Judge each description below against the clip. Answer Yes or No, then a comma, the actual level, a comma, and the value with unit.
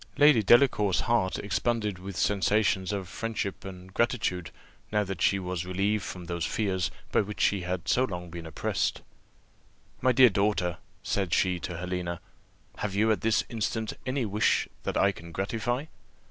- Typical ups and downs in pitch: Yes, average, 3.4 semitones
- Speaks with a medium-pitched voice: No, low, 100 Hz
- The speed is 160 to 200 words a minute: Yes, average, 165 wpm